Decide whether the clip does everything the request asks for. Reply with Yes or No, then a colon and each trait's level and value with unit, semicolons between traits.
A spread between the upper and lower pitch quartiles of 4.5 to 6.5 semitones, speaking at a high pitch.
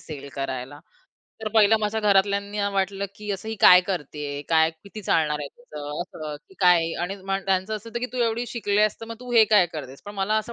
Yes: average, 5.1 semitones; high, 195 Hz